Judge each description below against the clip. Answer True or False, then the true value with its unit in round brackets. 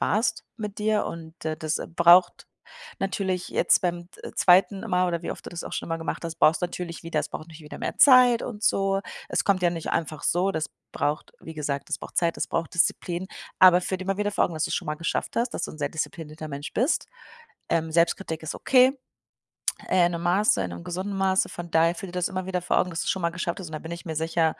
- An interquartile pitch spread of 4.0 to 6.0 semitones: False (2.7 semitones)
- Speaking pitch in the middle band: True (175 Hz)